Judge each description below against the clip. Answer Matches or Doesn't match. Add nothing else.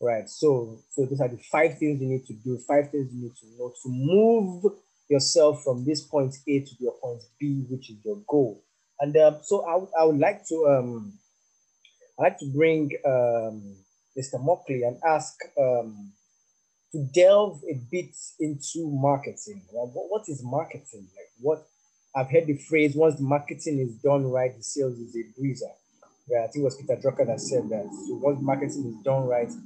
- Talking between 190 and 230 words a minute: Matches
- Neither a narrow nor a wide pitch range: Matches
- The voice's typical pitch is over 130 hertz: Matches